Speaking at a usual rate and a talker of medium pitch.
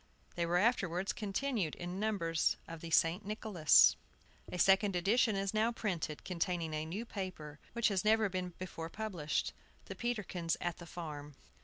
Yes: average, 160 wpm; medium, 180 Hz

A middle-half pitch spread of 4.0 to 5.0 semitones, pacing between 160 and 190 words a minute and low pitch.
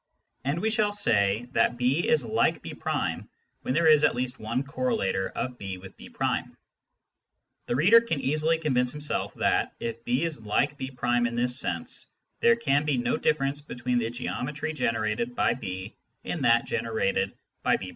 Yes: average, 4.5 semitones; average, 170 wpm; low, 125 Hz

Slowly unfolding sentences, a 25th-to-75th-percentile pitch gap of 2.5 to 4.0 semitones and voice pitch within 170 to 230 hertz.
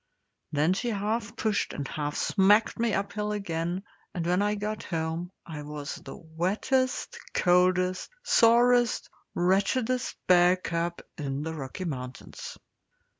No: slow, 125 wpm; average, 4.5 semitones; medium, 185 Hz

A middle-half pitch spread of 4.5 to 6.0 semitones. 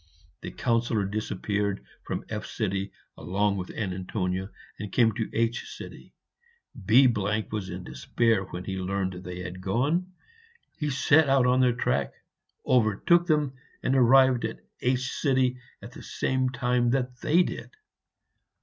Yes: average, 5.0 semitones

